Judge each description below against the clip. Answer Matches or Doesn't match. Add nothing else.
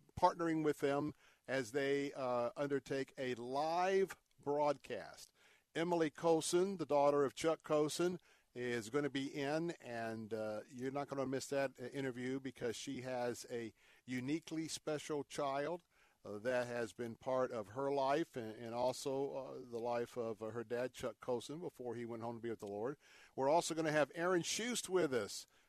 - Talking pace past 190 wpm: Doesn't match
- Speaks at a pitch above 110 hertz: Matches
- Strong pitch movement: Doesn't match